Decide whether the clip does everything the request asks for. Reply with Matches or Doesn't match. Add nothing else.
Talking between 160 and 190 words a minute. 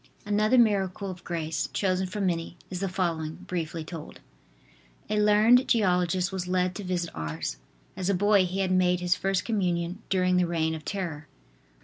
Matches